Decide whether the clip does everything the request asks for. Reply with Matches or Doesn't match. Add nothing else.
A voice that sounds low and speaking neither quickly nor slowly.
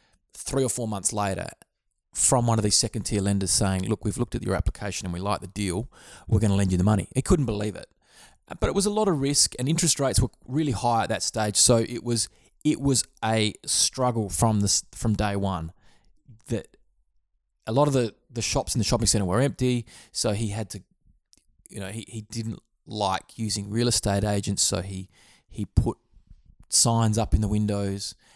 Doesn't match